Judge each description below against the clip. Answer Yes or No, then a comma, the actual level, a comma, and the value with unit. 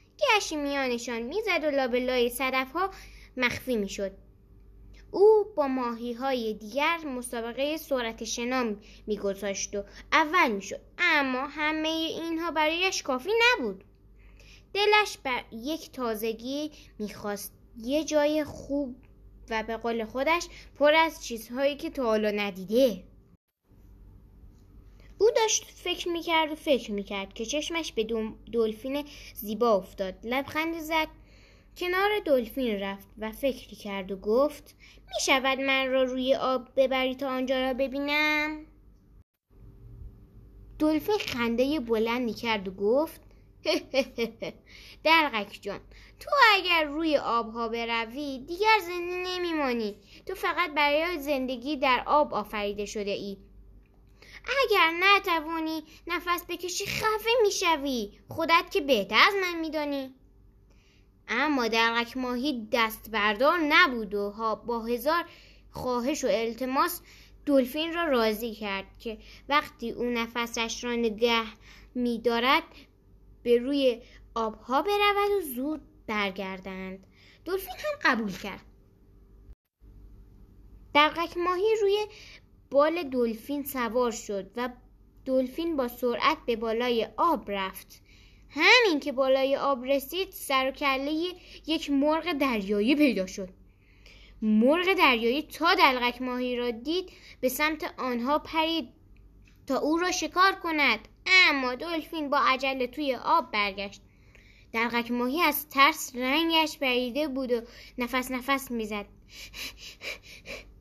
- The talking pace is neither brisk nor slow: Yes, average, 115 wpm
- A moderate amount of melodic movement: No, wide, 6.0 semitones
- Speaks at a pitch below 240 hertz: No, very high, 260 Hz